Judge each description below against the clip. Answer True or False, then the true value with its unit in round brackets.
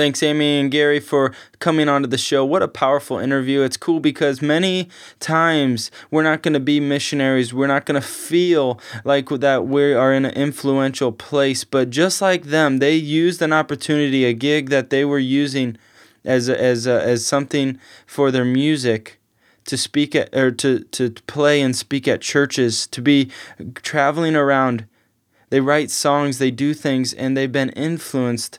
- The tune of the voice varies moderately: False (2.2 semitones)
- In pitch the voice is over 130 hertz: True (140 Hz)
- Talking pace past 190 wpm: False (175 wpm)